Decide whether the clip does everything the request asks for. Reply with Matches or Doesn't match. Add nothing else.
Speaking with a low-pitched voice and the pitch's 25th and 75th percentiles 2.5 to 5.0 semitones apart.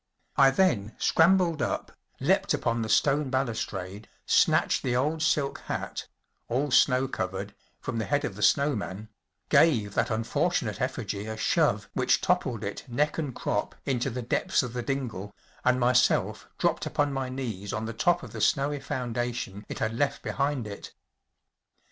Matches